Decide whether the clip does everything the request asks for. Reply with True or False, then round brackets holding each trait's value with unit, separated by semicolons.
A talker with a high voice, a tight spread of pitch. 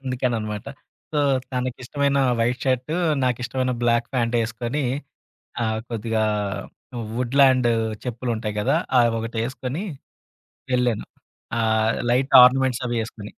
False (120 Hz; 2.1 semitones)